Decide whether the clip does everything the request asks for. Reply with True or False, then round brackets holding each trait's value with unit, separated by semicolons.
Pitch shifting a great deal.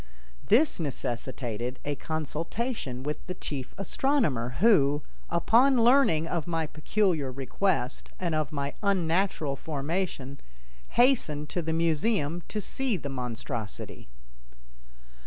True (6.2 semitones)